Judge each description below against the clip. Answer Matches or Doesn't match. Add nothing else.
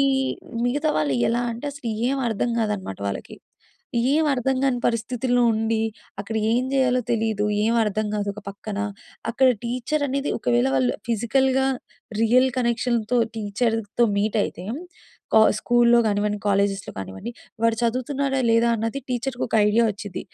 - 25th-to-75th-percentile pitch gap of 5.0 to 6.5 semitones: Doesn't match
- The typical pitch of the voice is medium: Doesn't match